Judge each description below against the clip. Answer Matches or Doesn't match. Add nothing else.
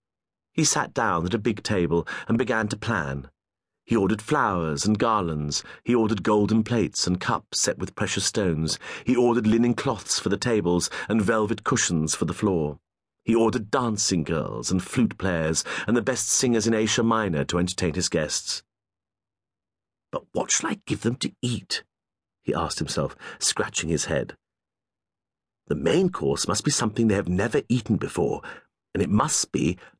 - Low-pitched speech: Matches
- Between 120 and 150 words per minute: Doesn't match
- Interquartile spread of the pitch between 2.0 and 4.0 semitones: Doesn't match